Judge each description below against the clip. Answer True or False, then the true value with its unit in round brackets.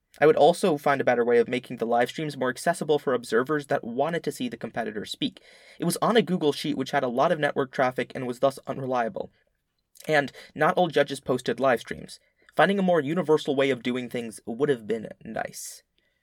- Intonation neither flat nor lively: True (3.5 semitones)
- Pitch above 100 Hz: True (140 Hz)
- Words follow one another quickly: True (220 wpm)